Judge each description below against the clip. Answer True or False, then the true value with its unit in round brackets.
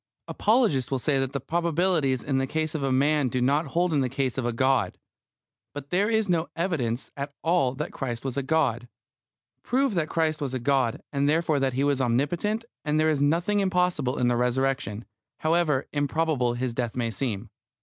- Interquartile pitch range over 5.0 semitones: False (4.1 semitones)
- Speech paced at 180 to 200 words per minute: True (190 wpm)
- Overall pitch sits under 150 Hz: True (140 Hz)